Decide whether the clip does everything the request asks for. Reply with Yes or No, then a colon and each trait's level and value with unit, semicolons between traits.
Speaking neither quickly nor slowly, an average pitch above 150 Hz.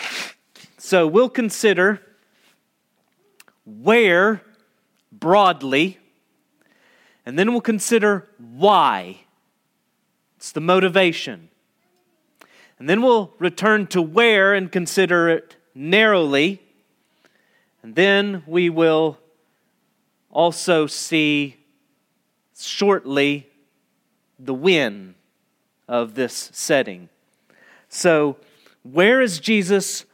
No: slow, 80 wpm; medium, 185 Hz